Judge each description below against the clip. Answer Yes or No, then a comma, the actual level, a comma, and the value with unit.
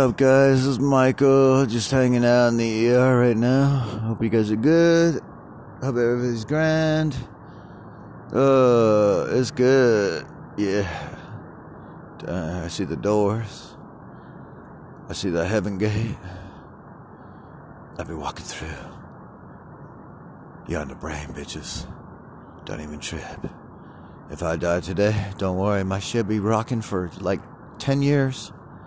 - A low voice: Yes, low, 115 Hz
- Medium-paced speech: No, slow, 130 wpm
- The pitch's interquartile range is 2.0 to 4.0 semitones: No, average, 5.1 semitones